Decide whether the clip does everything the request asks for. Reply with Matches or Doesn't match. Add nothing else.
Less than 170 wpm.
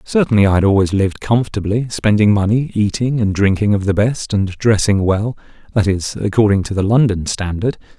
Doesn't match